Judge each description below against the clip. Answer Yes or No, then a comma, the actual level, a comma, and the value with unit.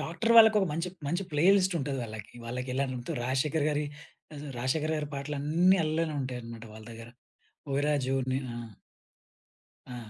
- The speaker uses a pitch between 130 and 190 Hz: Yes, medium, 140 Hz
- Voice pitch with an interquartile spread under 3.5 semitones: No, average, 4.1 semitones